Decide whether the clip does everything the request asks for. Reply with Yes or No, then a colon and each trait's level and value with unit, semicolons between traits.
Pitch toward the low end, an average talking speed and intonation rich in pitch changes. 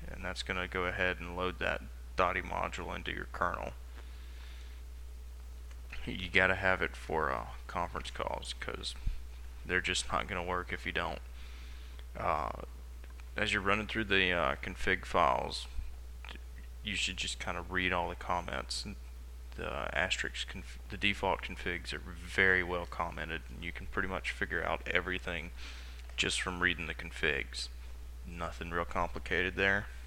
Yes: very low, 70 Hz; average, 155 wpm; wide, 6.5 semitones